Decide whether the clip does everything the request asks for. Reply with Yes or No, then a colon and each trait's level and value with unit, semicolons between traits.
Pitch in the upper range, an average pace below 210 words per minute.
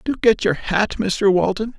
Yes: high, 200 Hz; average, 200 wpm